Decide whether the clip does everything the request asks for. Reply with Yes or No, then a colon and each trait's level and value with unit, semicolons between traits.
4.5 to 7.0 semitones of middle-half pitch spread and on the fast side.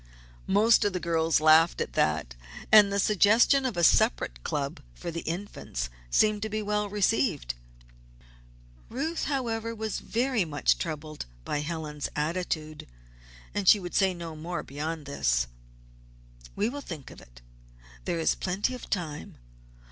No: wide, 5.6 semitones; average, 150 wpm